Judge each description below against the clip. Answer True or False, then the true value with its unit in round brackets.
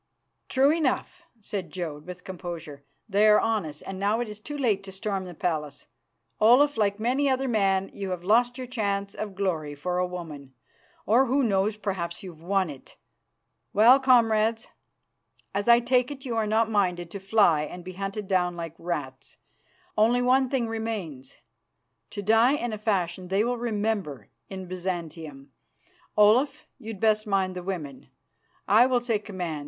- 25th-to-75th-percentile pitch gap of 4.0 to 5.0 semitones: True (4.3 semitones)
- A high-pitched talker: True (200 Hz)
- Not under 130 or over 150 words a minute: False (170 wpm)